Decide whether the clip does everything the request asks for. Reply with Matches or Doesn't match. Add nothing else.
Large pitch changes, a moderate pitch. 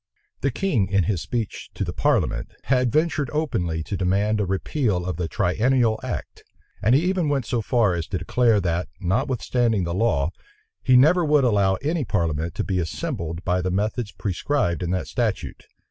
Doesn't match